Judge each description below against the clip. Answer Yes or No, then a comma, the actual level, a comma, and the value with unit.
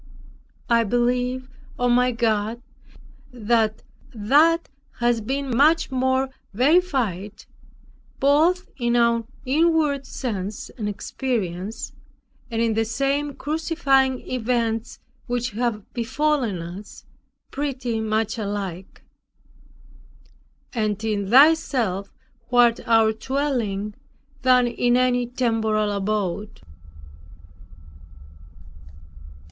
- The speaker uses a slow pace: Yes, slow, 90 wpm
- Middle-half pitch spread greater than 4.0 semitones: No, average, 3.6 semitones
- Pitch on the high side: Yes, high, 240 Hz